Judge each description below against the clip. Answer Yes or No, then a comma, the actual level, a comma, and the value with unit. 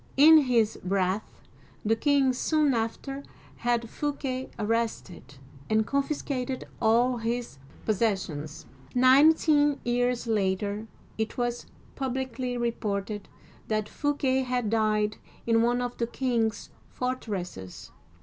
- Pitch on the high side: Yes, high, 235 Hz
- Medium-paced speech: No, slow, 105 wpm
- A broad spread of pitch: No, average, 3.3 semitones